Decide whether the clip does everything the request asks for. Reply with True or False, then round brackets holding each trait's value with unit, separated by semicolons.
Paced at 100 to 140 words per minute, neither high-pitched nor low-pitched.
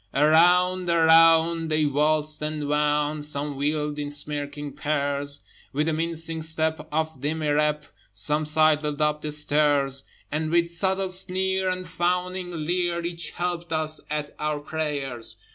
True (135 wpm; 155 Hz)